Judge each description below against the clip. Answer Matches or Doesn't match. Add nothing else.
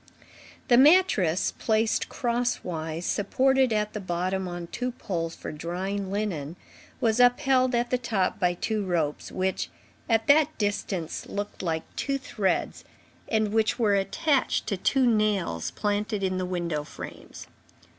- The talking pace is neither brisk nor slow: Matches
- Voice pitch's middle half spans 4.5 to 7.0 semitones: Matches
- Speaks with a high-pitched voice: Matches